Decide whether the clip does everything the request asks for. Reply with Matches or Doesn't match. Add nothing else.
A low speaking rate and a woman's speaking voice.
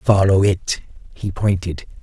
Doesn't match